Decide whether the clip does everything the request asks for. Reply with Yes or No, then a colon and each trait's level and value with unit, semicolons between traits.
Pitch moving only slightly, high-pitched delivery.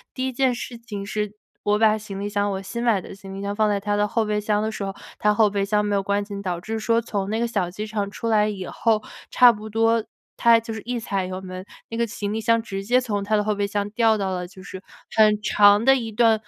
Yes: narrow, 2.0 semitones; high, 210 Hz